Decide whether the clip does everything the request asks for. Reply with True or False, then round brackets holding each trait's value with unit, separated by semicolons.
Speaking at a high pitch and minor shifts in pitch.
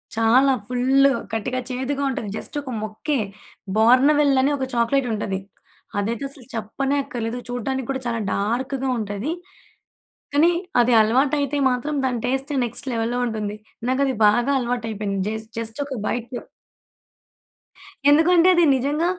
False (250 Hz; 3.4 semitones)